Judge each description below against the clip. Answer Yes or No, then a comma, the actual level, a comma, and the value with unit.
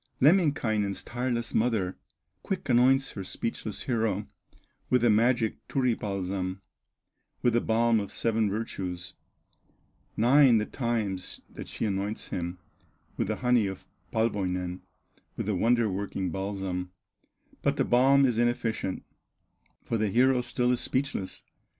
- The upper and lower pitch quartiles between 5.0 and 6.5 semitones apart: No, average, 4.0 semitones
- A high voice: No, low, 110 Hz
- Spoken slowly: Yes, slow, 130 wpm